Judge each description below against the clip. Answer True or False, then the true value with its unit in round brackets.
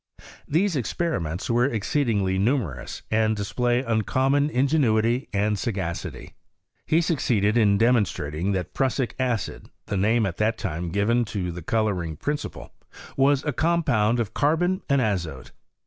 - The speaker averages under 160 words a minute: True (145 wpm)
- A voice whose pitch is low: True (110 Hz)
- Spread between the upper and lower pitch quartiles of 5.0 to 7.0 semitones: True (5.3 semitones)